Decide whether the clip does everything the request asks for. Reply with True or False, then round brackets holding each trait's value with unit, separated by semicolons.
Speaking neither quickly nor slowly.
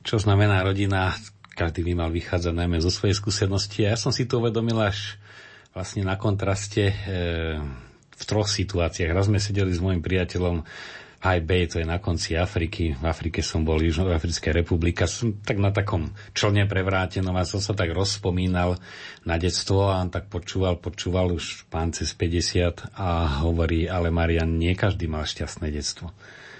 False (175 wpm)